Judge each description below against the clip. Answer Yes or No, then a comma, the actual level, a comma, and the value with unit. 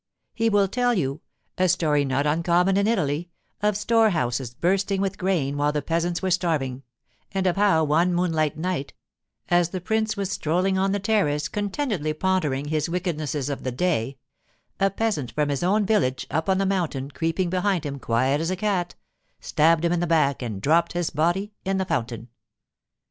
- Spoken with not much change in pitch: No, average, 4.7 semitones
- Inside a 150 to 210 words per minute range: Yes, average, 175 wpm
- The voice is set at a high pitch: No, medium, 170 Hz